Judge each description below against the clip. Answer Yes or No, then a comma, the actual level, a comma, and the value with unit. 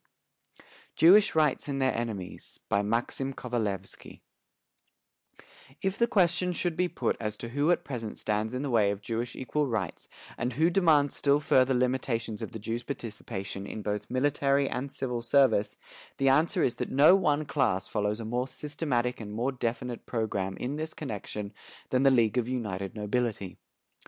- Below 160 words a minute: No, average, 170 wpm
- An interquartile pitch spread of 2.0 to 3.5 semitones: No, average, 4.5 semitones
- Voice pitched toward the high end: No, low, 125 Hz